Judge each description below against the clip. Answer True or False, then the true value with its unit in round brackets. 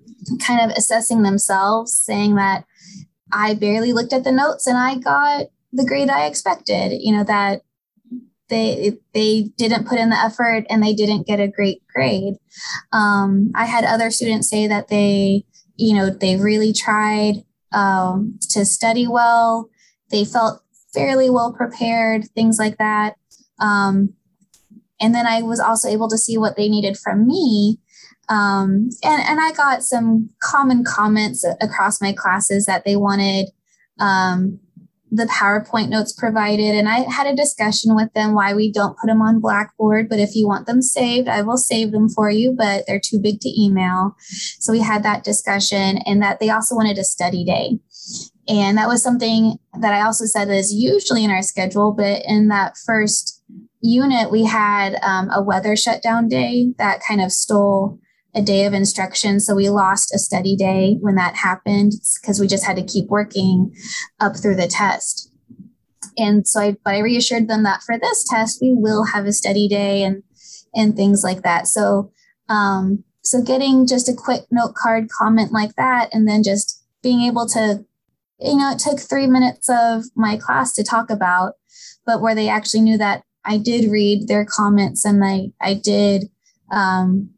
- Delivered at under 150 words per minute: False (180 wpm)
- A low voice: False (215 Hz)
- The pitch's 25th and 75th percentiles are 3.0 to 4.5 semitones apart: False (2.4 semitones)